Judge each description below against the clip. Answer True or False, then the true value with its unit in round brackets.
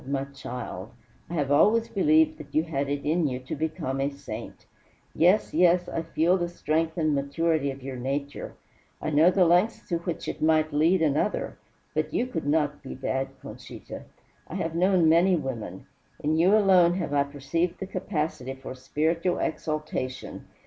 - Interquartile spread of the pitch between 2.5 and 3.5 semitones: False (3.9 semitones)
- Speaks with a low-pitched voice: False (155 Hz)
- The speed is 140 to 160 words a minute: False (175 wpm)